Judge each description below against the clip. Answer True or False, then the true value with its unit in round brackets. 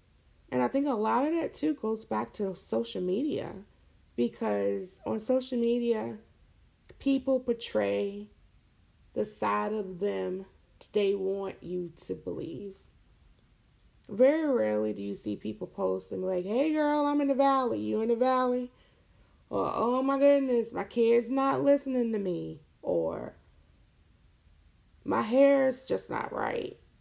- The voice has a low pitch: False (195 Hz)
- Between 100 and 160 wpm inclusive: True (140 wpm)